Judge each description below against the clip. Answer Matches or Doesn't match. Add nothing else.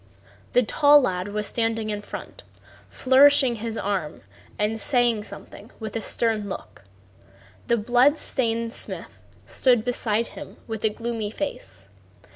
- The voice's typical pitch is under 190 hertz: Doesn't match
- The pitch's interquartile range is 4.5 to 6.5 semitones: Doesn't match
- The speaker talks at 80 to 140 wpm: Matches